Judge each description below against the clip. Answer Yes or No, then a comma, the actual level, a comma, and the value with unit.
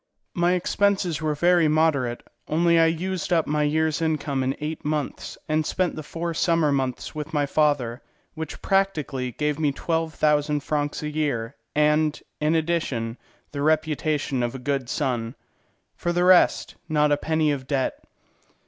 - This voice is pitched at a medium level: Yes, medium, 150 Hz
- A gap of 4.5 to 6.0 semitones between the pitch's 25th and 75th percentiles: No, narrow, 2.4 semitones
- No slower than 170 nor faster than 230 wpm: No, average, 160 wpm